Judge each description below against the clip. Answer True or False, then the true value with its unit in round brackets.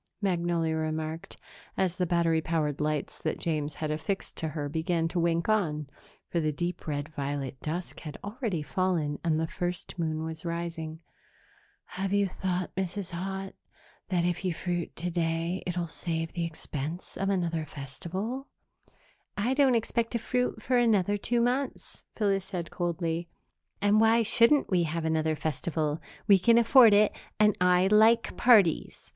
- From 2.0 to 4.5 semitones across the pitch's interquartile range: True (3.8 semitones)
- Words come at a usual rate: True (160 wpm)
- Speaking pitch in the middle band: True (175 Hz)